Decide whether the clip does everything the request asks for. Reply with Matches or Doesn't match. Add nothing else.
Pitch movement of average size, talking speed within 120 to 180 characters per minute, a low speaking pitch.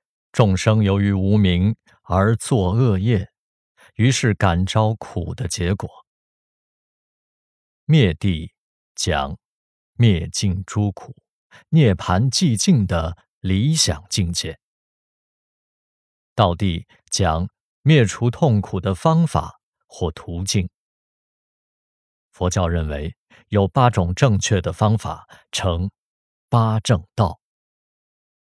Matches